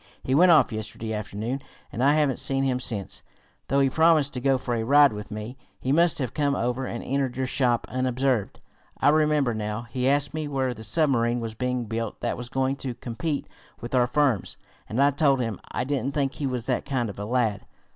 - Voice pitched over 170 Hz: No, low, 130 Hz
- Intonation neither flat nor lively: Yes, average, 3.1 semitones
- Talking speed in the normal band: No, fast, 220 wpm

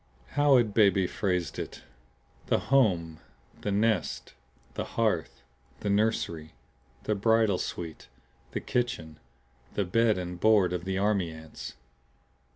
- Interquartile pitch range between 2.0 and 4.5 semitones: Yes, average, 4.1 semitones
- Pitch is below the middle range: Yes, low, 100 Hz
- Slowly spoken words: Yes, slow, 130 wpm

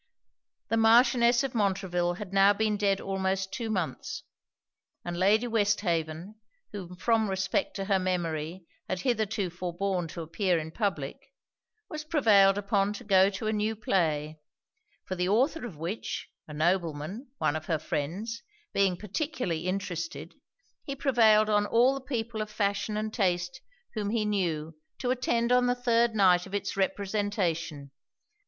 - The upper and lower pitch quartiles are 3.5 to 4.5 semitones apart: Yes, average, 3.9 semitones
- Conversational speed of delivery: Yes, average, 150 wpm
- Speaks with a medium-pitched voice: No, high, 200 Hz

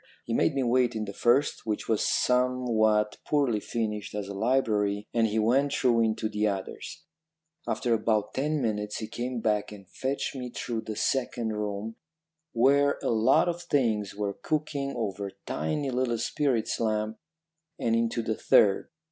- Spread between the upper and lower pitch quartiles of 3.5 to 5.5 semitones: No, average, 3.1 semitones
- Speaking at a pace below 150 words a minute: No, average, 165 wpm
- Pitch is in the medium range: No, low, 115 Hz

